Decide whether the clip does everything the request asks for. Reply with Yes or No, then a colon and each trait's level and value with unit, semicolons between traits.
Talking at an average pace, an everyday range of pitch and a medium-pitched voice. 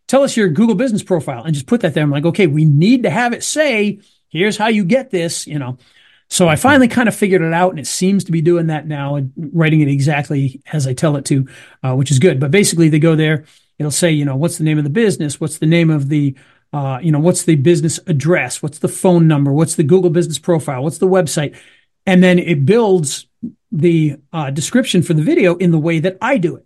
No: fast, 250 wpm; average, 3.9 semitones; medium, 165 Hz